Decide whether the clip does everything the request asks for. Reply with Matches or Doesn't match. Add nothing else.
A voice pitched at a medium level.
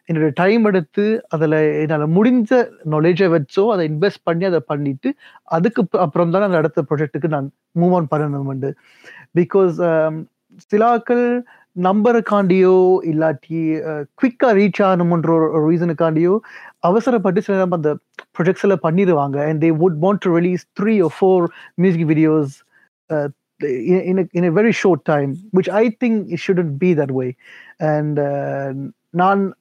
Matches